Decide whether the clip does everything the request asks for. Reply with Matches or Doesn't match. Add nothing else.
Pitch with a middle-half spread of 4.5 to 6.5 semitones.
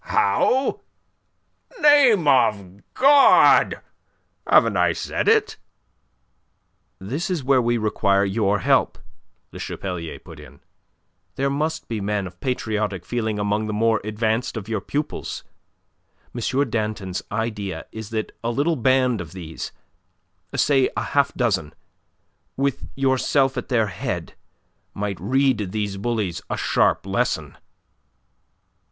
Matches